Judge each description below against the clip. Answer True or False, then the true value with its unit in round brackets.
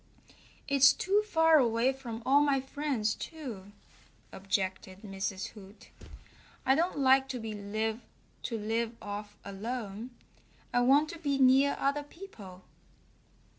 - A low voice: False (245 Hz)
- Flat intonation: False (5.2 semitones)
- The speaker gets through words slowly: True (115 wpm)